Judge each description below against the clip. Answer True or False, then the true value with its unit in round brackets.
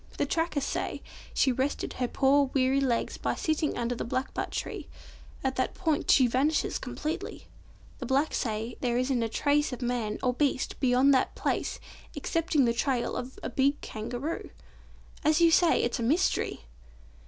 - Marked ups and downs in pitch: False (3.2 semitones)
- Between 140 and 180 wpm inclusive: True (165 wpm)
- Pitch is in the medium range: False (265 Hz)